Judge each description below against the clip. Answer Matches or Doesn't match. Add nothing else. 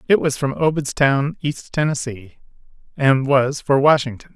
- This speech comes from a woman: Doesn't match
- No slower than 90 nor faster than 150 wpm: Matches